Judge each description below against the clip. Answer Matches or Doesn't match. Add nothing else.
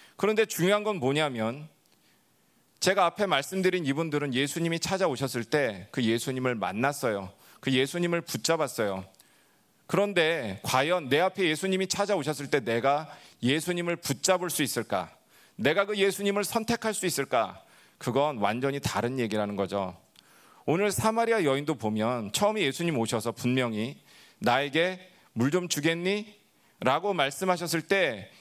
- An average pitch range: Doesn't match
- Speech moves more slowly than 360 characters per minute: Matches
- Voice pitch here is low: Doesn't match